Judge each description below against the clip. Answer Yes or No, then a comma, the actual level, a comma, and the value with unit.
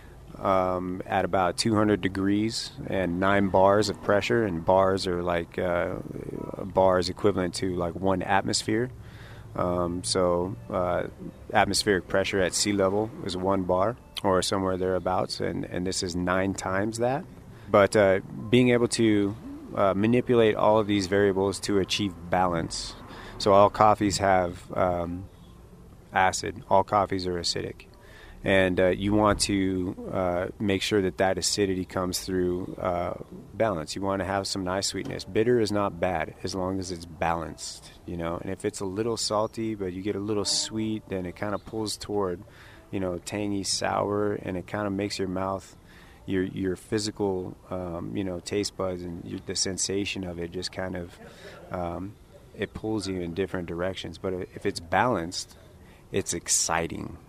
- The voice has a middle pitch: No, very low, 95 Hz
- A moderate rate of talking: Yes, average, 165 wpm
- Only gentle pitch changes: Yes, narrow, 2.3 semitones